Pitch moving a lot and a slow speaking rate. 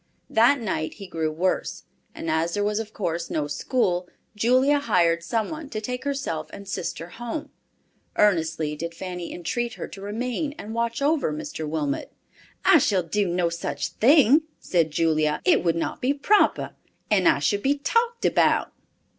No: wide, 7.3 semitones; average, 170 wpm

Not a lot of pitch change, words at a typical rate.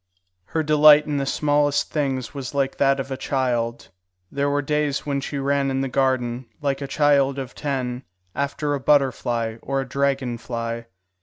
Yes: narrow, 1.8 semitones; average, 175 wpm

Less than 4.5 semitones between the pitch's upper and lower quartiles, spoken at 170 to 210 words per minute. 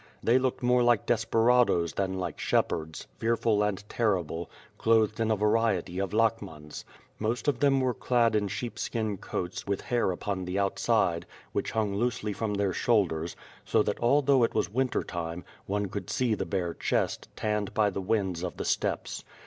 Yes: average, 3.8 semitones; average, 175 wpm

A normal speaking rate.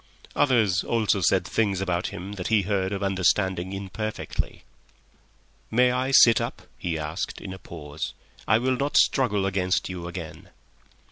Yes: average, 150 wpm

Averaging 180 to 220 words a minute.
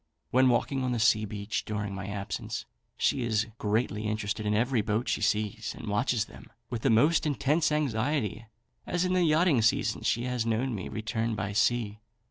Yes: average, 185 wpm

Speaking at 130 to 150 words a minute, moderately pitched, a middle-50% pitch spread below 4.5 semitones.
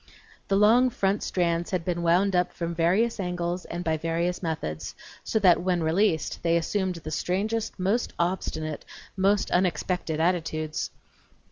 Yes: average, 145 wpm; medium, 180 Hz; narrow, 2.5 semitones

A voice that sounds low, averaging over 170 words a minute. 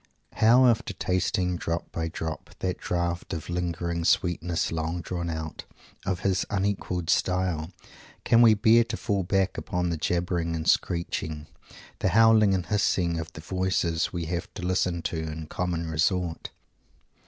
No: very low, 90 Hz; average, 155 wpm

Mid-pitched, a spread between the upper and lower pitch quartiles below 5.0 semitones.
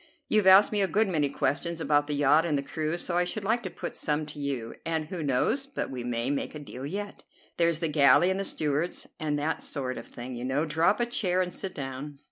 Yes: medium, 155 Hz; average, 4.4 semitones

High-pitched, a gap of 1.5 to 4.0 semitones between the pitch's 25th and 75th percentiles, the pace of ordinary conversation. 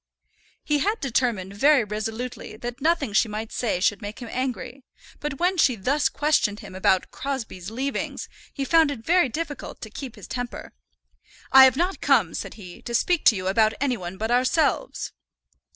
No: high, 245 Hz; average, 4.9 semitones; average, 180 wpm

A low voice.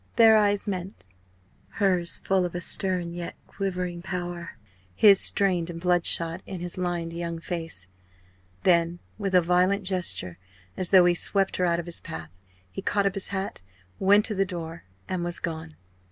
No: medium, 180 Hz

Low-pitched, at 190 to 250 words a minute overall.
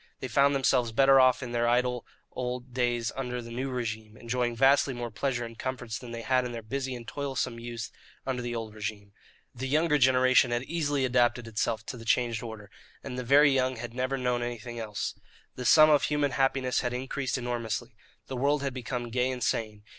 Yes: low, 125 Hz; fast, 205 wpm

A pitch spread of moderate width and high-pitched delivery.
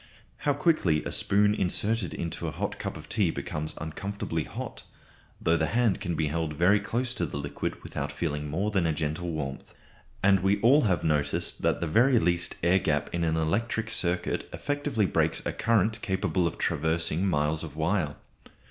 No: average, 4.8 semitones; very low, 85 Hz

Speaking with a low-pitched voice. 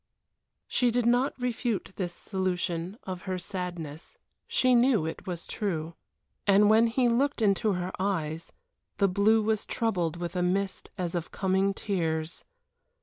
No: high, 190 Hz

